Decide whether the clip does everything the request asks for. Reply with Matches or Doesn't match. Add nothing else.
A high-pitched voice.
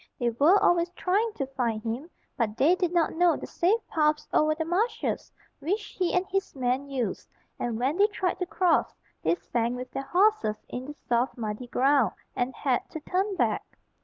Matches